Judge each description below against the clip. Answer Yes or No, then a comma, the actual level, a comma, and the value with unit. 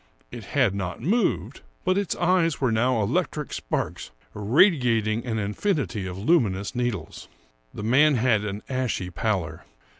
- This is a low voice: Yes, low, 115 Hz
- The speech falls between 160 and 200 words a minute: No, average, 140 wpm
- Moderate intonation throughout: No, wide, 6.4 semitones